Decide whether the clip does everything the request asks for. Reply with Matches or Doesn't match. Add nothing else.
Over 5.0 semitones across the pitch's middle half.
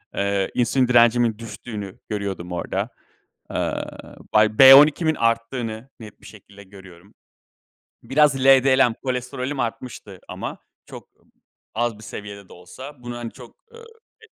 Doesn't match